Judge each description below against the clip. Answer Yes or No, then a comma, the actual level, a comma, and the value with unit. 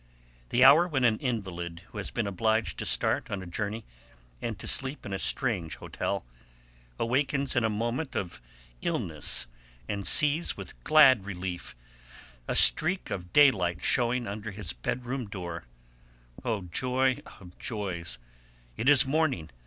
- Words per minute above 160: No, average, 145 wpm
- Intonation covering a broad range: Yes, wide, 6.1 semitones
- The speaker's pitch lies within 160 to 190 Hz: No, low, 110 Hz